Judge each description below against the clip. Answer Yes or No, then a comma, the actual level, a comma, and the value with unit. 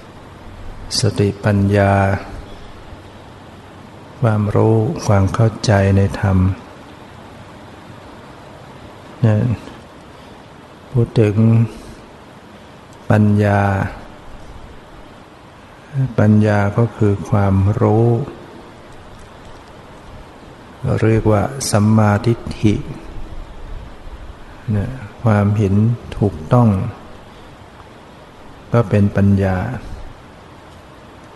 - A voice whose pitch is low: Yes, low, 105 Hz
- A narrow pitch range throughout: Yes, narrow, 2.3 semitones